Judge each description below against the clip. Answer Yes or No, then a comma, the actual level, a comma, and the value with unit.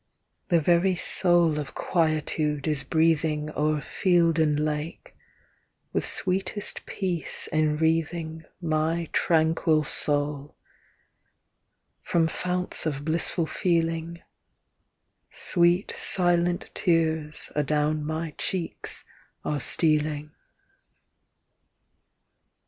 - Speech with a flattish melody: Yes, narrow, 2.1 semitones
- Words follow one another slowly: Yes, slow, 80 wpm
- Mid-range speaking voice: Yes, medium, 160 Hz